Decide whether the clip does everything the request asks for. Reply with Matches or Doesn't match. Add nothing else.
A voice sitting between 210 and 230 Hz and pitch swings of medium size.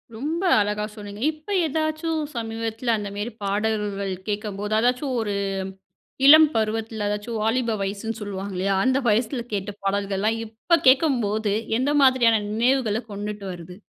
Matches